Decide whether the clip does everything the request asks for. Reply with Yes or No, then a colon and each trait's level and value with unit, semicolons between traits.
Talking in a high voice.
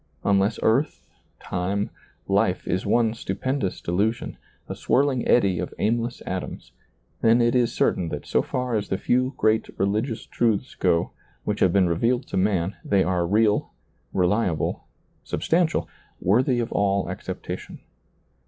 No: low, 105 Hz